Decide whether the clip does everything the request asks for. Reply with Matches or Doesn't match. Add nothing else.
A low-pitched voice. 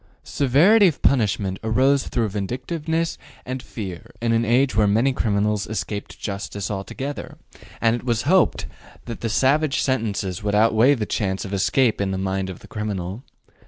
Matches